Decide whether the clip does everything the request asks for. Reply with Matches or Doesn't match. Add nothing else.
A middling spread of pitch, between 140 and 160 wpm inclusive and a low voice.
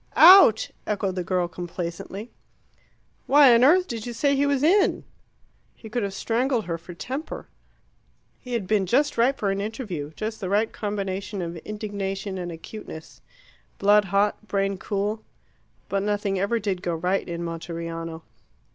Doesn't match